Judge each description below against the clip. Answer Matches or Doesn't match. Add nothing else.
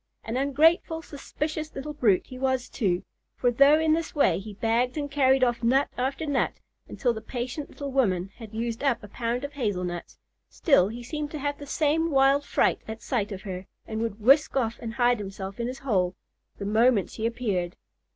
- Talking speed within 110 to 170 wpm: Doesn't match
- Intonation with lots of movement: Doesn't match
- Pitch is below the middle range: Doesn't match